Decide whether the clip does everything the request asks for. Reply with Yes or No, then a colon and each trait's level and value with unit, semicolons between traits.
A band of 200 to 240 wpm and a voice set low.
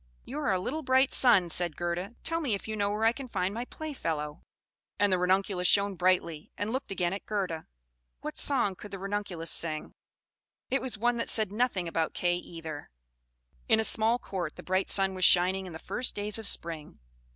No: fast, 205 wpm; high, 195 Hz